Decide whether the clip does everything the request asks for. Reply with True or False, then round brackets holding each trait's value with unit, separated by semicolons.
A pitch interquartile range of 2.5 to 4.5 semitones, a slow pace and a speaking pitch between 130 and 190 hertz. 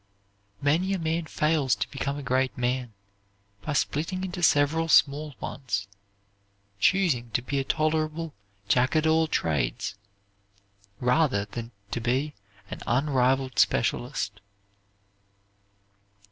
True (4.2 semitones; 115 wpm; 140 Hz)